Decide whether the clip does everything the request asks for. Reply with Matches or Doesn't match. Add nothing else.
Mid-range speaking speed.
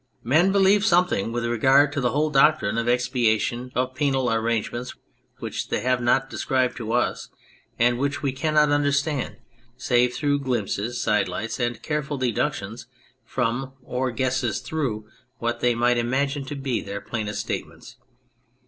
Matches